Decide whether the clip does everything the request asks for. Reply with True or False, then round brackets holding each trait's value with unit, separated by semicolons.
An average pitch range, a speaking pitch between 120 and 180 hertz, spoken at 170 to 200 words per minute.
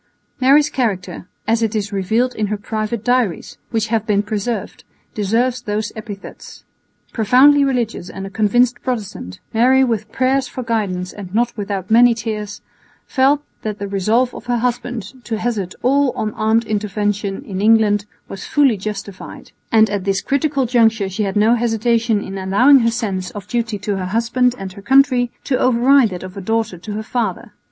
False (3.2 semitones; 220 Hz; 175 wpm)